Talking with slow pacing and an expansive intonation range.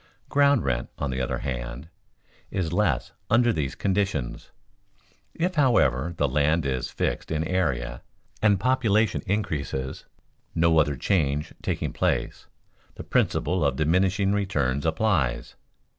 Yes: slow, 125 wpm; wide, 6.8 semitones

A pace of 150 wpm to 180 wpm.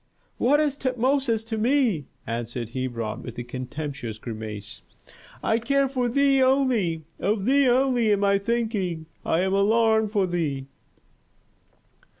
No: slow, 135 wpm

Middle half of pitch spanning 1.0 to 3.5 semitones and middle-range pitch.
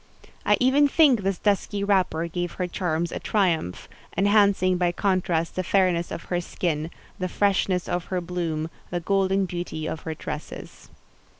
Yes: narrow, 2.6 semitones; medium, 180 Hz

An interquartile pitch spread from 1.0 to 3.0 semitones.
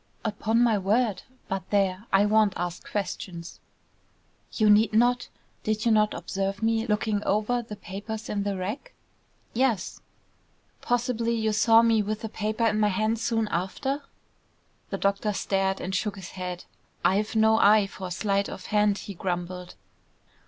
Yes: narrow, 2.4 semitones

